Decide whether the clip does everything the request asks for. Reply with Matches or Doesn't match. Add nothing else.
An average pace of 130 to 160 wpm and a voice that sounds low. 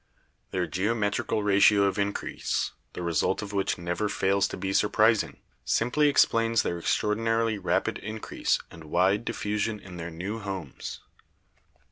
Matches